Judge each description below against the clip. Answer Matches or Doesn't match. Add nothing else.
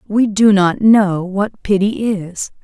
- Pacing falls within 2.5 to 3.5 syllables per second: Matches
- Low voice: Doesn't match